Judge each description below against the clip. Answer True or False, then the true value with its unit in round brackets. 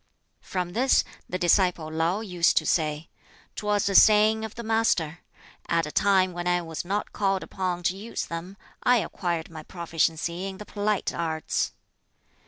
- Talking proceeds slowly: False (165 wpm)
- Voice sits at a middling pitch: True (180 Hz)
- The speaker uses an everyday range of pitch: True (3.5 semitones)